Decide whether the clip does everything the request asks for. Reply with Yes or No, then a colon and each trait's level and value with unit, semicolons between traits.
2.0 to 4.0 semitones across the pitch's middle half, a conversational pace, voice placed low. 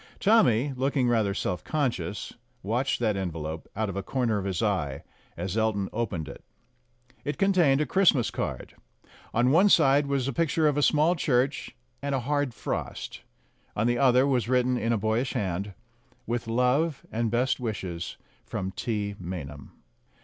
No: wide, 5.5 semitones; average, 165 wpm; low, 120 Hz